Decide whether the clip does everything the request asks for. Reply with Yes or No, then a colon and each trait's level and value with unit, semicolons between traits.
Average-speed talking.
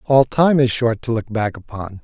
No: fast, 235 wpm